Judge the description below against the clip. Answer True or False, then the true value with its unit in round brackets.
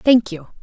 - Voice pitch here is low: False (210 Hz)